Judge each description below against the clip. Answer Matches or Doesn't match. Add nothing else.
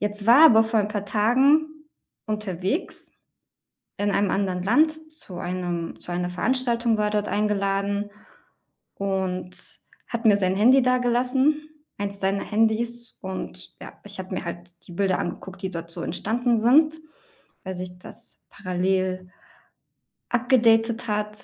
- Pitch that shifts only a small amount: Doesn't match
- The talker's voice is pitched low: Doesn't match